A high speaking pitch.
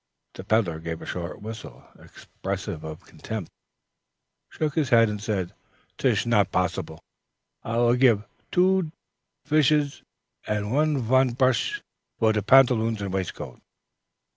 No: low, 115 Hz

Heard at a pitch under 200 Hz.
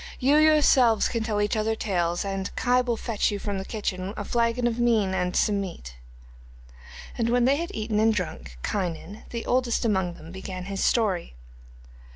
No: high, 210 Hz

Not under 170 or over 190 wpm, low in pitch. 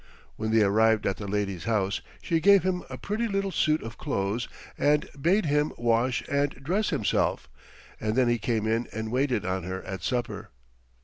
Yes: average, 185 wpm; low, 120 Hz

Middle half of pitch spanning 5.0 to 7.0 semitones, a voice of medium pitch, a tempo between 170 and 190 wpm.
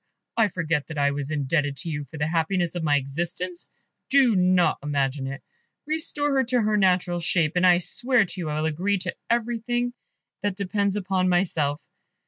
Yes: average, 5.3 semitones; medium, 180 Hz; average, 185 wpm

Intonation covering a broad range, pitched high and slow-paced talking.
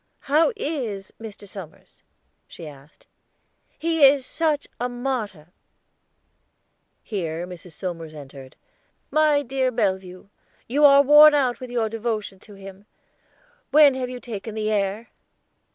Yes: wide, 6.3 semitones; high, 225 Hz; slow, 125 wpm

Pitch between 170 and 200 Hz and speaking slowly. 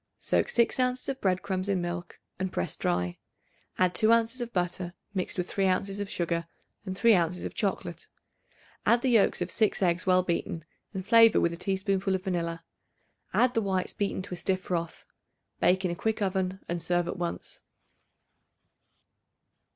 No: medium, 185 Hz; average, 180 wpm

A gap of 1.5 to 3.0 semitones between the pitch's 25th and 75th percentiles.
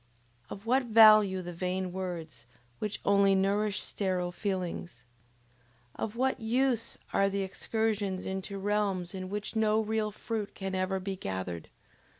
Yes: narrow, 2.5 semitones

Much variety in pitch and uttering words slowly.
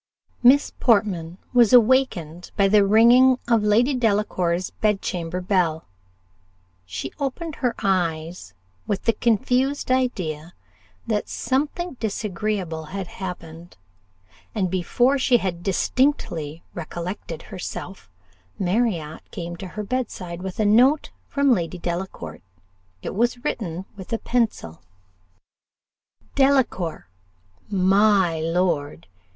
Yes: wide, 5.8 semitones; slow, 105 wpm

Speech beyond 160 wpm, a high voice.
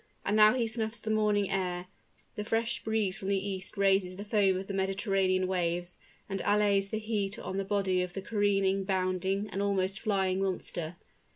Yes: average, 185 wpm; high, 195 Hz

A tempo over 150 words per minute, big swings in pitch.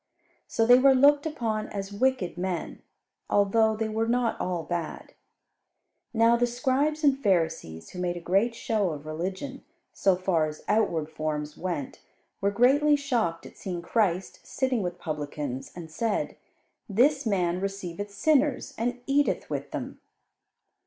No: average, 145 wpm; wide, 6.1 semitones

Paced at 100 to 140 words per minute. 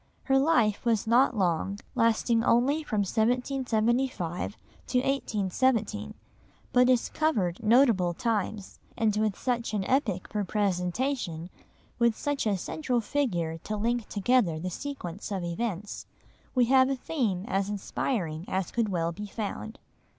Yes: slow, 135 wpm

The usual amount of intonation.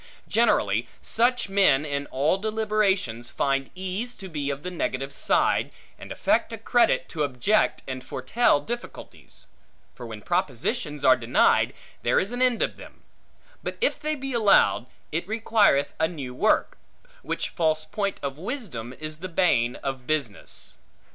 No: wide, 7.8 semitones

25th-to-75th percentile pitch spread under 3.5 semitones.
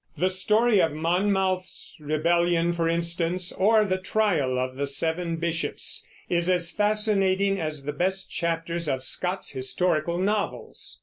Yes: average, 2.7 semitones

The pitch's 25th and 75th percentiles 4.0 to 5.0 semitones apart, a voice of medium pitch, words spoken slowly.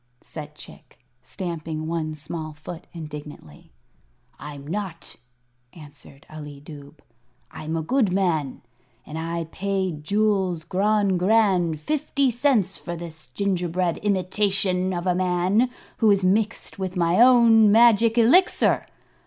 Yes: average, 4.6 semitones; medium, 180 Hz; slow, 120 wpm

